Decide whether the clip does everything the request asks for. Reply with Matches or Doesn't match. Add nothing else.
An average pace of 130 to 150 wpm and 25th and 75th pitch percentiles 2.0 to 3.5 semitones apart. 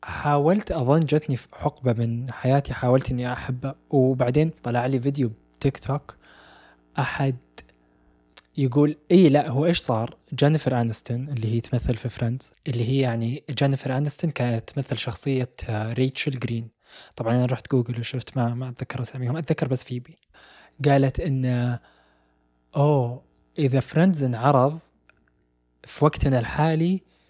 Matches